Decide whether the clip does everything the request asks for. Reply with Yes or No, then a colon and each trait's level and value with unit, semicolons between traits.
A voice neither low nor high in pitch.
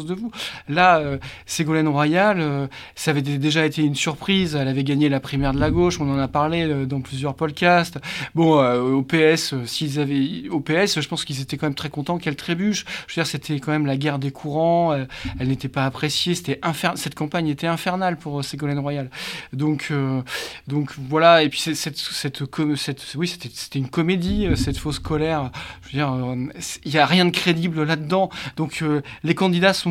Yes: medium, 150 Hz